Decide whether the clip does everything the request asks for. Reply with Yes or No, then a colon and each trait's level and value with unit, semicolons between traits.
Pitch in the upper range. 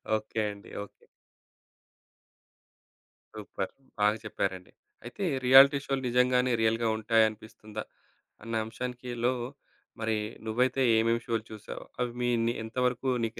No: low, 115 Hz